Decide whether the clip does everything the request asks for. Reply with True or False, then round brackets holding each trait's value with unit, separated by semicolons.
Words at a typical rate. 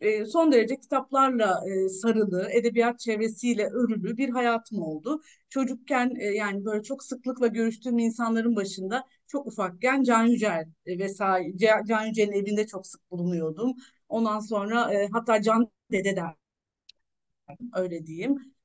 True (115 wpm)